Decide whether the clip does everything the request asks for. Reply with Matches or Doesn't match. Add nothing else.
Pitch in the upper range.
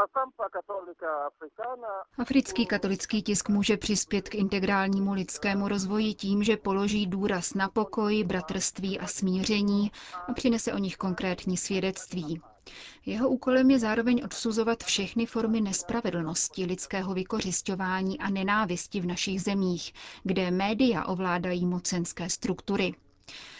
Matches